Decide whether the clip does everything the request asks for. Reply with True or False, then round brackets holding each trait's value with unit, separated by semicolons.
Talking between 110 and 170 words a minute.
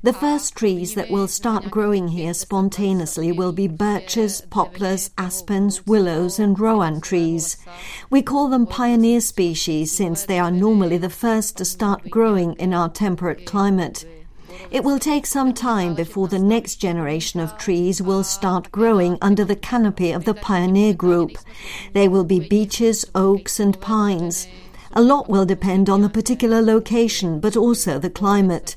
True (160 wpm)